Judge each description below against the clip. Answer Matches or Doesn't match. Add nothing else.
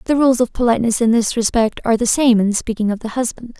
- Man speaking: Doesn't match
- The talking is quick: Matches